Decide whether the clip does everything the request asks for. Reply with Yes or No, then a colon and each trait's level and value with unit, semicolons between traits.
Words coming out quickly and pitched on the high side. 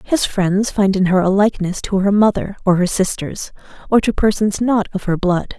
Yes: fast, 215 wpm; high, 195 Hz